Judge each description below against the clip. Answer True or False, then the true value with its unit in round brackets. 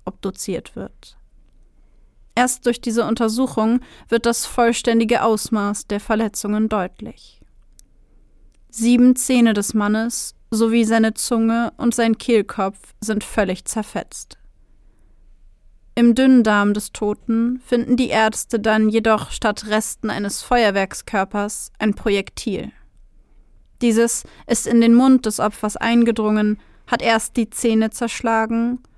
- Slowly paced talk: True (115 wpm)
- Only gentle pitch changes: True (1.9 semitones)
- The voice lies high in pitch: True (225 Hz)